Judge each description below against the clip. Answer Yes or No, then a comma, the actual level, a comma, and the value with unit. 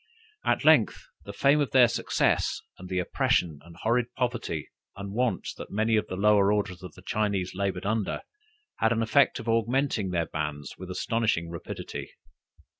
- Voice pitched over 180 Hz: No, low, 105 Hz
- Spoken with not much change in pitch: No, average, 4.1 semitones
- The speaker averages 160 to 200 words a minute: Yes, average, 165 wpm